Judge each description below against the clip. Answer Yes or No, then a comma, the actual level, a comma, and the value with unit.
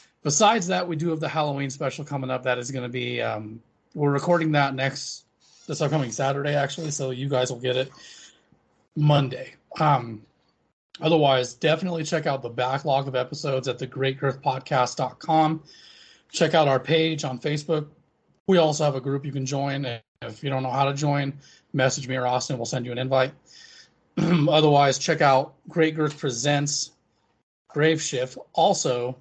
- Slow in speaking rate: No, average, 170 wpm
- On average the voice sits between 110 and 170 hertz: Yes, medium, 140 Hz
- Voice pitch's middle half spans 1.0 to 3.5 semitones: Yes, average, 3.0 semitones